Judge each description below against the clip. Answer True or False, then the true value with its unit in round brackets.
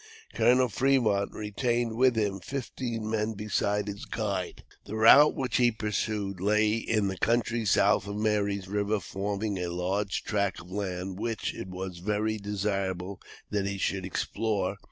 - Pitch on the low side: True (105 Hz)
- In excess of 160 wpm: False (155 wpm)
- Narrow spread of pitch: True (2.2 semitones)